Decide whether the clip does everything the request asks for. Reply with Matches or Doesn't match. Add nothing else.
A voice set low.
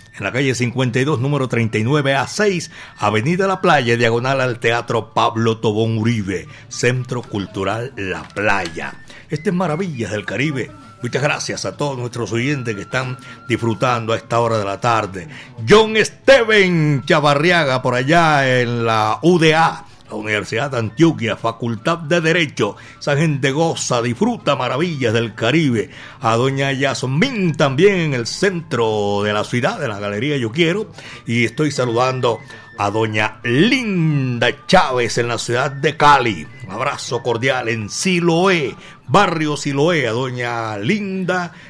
Matches